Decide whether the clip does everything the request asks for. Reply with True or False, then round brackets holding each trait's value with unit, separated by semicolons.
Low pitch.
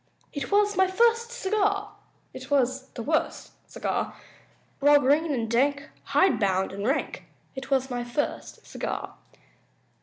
False (285 Hz)